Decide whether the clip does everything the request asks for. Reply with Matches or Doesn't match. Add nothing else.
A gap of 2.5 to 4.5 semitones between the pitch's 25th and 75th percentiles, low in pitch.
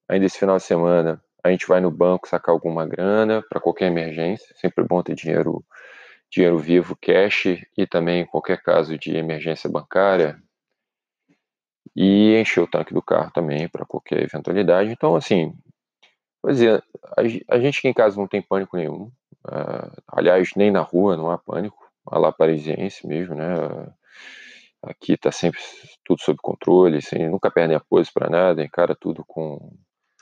Matches